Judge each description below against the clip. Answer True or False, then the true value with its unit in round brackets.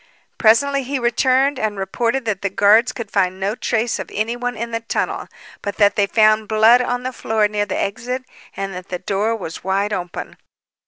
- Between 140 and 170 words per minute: False (195 wpm)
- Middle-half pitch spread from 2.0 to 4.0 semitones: True (3.4 semitones)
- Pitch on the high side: True (220 Hz)